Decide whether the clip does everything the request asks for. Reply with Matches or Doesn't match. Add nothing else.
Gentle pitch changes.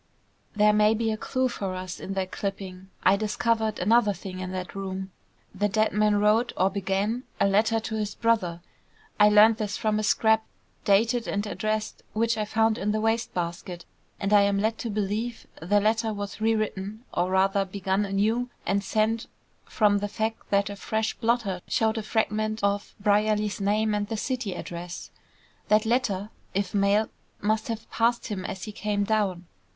Matches